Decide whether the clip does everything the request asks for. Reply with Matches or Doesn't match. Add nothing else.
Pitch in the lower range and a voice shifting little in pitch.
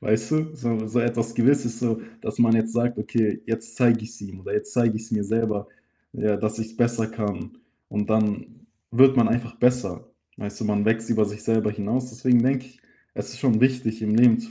Matches